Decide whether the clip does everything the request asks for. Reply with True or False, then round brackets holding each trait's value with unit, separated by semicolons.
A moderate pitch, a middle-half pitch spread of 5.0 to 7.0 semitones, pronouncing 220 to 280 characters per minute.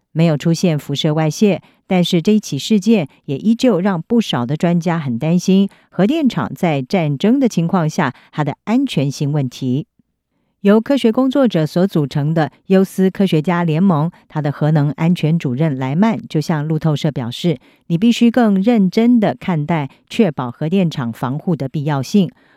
True (170 Hz; 5.3 semitones; 260 characters per minute)